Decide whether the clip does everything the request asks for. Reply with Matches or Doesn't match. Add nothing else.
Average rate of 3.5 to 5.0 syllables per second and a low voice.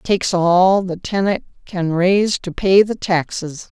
Doesn't match